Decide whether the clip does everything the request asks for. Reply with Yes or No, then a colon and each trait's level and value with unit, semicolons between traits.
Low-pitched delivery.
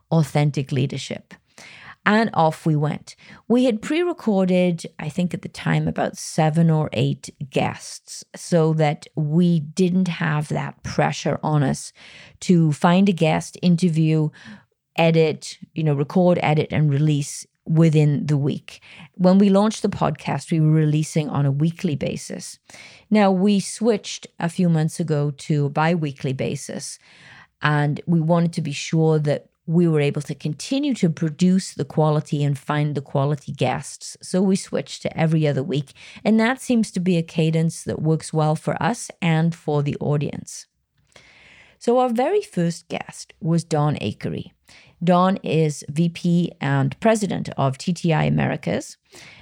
No: medium, 160 Hz